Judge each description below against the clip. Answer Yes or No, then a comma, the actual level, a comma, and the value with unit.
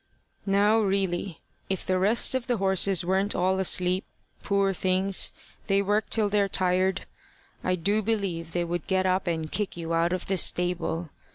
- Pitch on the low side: No, high, 190 Hz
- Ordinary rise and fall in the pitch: No, narrow, 1.9 semitones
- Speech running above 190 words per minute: No, average, 170 wpm